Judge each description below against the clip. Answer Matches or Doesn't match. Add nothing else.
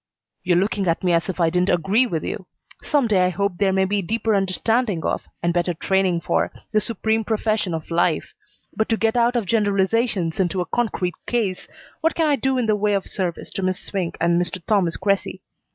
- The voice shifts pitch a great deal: Doesn't match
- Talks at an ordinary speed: Doesn't match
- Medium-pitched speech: Doesn't match